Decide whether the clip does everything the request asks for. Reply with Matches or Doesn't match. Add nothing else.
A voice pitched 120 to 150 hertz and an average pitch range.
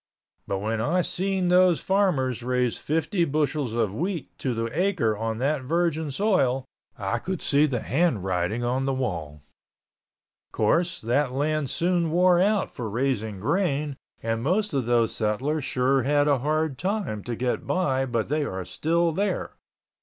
Doesn't match